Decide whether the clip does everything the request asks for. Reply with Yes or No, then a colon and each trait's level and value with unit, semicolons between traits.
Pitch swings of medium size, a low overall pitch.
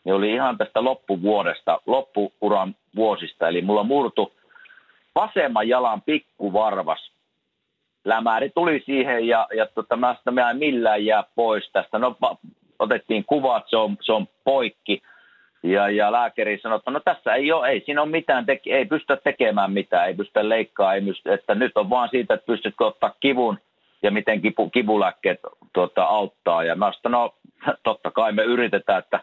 Yes: average, 3.6 semitones; low, 110 Hz